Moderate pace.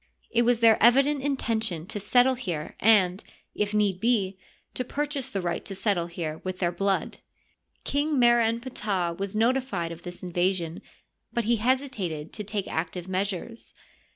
Yes: average, 160 wpm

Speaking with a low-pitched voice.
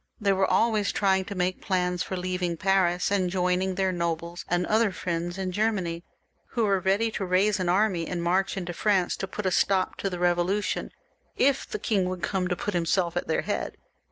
No: medium, 185 Hz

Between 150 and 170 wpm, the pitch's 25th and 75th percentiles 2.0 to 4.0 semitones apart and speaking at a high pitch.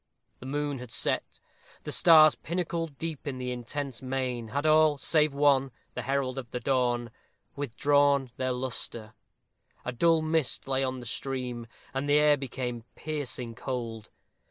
No: average, 155 wpm; average, 2.8 semitones; low, 135 Hz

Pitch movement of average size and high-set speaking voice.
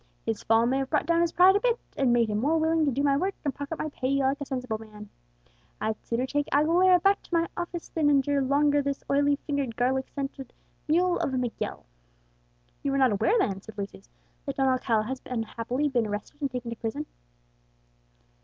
Yes: average, 3.9 semitones; very high, 275 Hz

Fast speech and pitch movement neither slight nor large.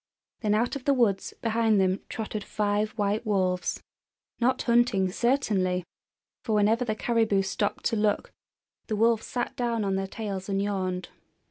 No: average, 155 wpm; average, 3.0 semitones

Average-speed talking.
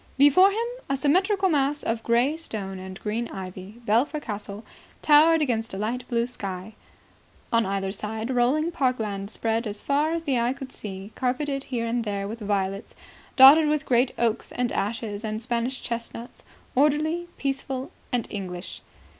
Yes: average, 165 wpm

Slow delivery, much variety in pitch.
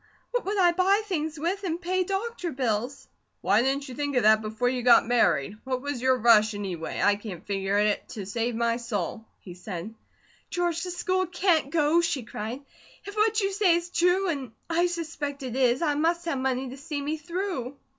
No: fast, 205 wpm; wide, 7.1 semitones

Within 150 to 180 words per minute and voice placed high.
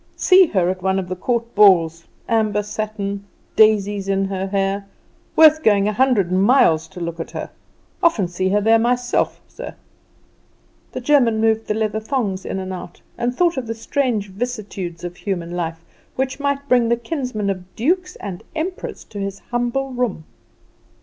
Yes: average, 170 wpm; high, 210 Hz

